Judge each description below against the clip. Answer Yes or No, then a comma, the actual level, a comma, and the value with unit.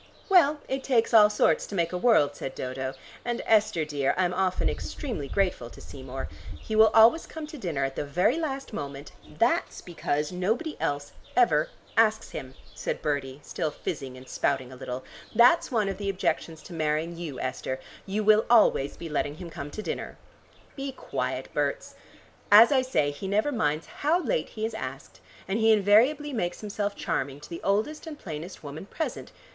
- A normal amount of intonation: No, wide, 7.8 semitones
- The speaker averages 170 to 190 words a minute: Yes, average, 185 wpm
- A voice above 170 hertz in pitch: Yes, medium, 185 Hz